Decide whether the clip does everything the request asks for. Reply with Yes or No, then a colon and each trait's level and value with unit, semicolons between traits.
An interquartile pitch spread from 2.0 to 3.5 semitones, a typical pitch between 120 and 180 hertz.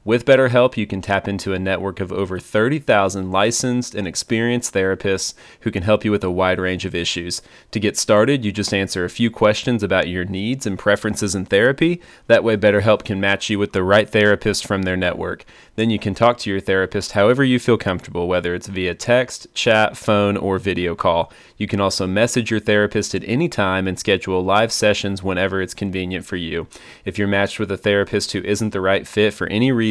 No: narrow, 2.4 semitones; low, 100 Hz